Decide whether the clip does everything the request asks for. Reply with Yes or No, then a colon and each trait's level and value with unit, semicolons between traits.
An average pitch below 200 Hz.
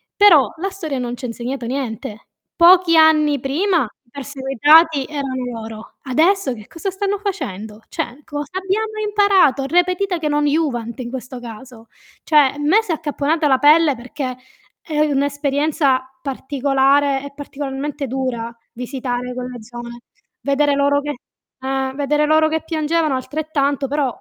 No: very high, 285 Hz